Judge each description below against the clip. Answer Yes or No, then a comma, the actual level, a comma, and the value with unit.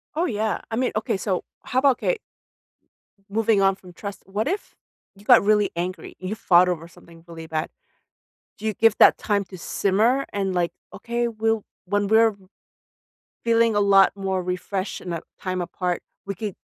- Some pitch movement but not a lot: Yes, average, 3.4 semitones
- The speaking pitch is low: No, high, 200 Hz